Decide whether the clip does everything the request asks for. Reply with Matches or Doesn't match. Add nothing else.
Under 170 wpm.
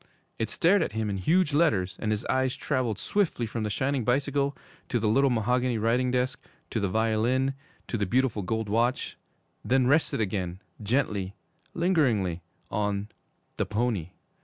Matches